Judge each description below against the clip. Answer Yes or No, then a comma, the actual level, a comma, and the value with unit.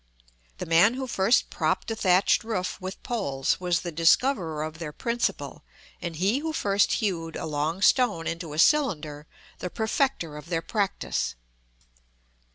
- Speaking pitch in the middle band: Yes, medium, 180 Hz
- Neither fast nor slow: Yes, average, 155 wpm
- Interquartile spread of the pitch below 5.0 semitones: No, wide, 5.5 semitones